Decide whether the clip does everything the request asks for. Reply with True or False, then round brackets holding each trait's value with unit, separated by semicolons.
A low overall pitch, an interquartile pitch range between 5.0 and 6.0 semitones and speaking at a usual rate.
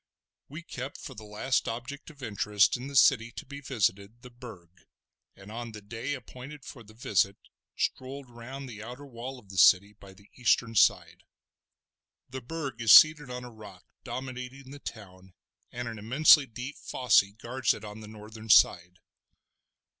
False (120 Hz; 3.8 semitones; 170 wpm)